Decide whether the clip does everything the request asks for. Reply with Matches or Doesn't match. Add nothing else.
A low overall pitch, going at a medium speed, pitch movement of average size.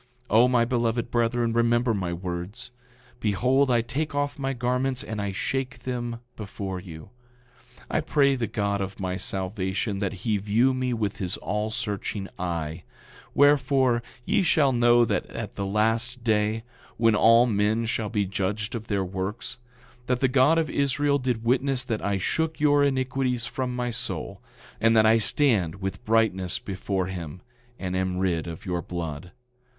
Matches